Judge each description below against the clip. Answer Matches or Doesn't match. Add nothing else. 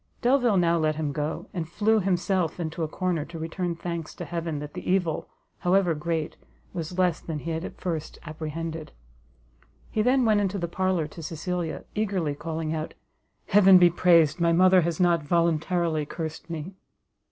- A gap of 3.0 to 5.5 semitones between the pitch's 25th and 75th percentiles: Doesn't match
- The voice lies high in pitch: Doesn't match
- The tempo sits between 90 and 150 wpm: Doesn't match